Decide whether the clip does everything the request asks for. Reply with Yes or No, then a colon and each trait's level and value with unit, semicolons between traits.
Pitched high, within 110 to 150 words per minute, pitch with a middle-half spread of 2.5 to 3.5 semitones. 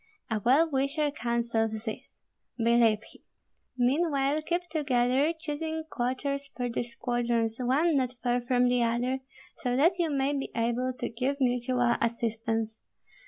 Yes: very high, 250 Hz; average, 140 wpm; average, 3.1 semitones